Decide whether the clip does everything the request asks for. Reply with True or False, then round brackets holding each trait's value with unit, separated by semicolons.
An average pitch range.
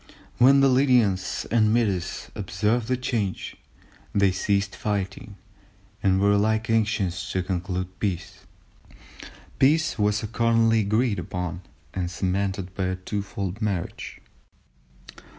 True (3.2 semitones)